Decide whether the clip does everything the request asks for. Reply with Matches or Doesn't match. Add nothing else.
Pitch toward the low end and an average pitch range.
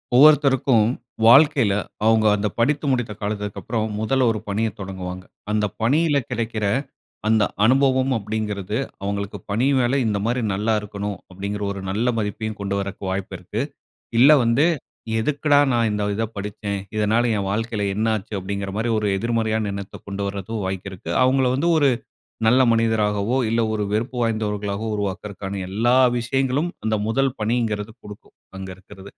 Matches